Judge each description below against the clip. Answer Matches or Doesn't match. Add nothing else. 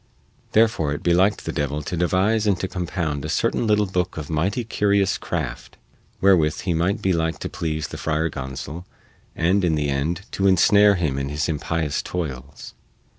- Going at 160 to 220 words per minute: Matches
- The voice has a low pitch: Matches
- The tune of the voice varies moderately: Matches